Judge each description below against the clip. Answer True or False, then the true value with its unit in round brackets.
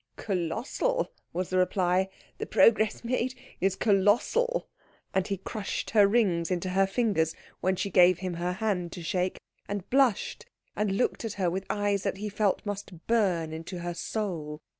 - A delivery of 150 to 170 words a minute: True (165 wpm)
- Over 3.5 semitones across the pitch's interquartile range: False (3.1 semitones)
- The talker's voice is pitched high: True (195 Hz)